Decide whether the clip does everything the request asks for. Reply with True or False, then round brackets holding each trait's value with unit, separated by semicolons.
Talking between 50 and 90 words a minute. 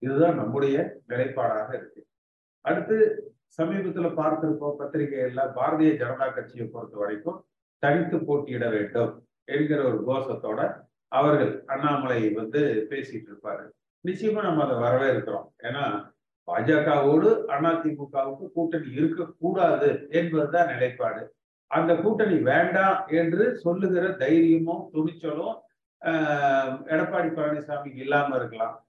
False (100 wpm)